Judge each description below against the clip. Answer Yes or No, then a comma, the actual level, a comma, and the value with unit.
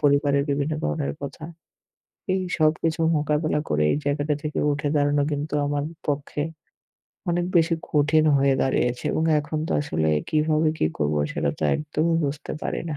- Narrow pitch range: Yes, narrow, 1.6 semitones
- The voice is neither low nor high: Yes, medium, 150 Hz